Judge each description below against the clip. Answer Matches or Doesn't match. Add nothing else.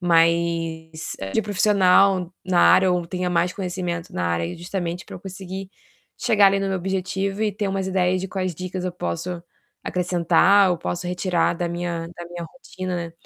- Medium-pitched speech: Matches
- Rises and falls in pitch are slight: Matches